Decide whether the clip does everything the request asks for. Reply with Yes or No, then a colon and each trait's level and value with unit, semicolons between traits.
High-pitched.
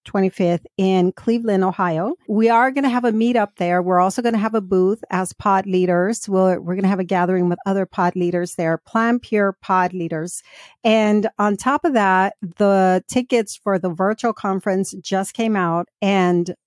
Yes: high, 195 Hz